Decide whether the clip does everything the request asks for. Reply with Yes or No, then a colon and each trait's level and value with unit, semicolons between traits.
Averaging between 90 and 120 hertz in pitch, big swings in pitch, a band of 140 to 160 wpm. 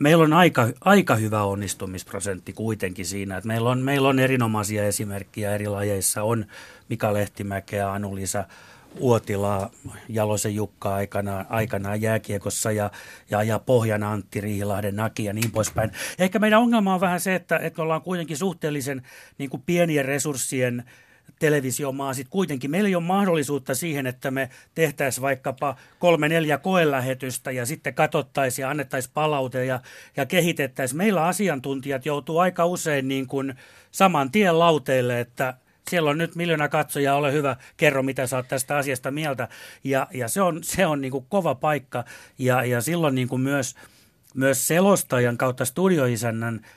No: low, 135 Hz; wide, 5.8 semitones; average, 150 wpm